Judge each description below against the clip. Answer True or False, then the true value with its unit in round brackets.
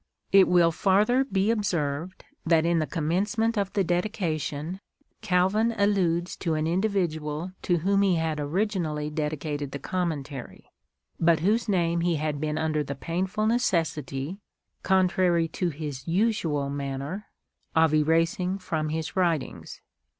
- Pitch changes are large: False (3.8 semitones)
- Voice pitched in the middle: True (170 Hz)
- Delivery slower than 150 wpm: True (140 wpm)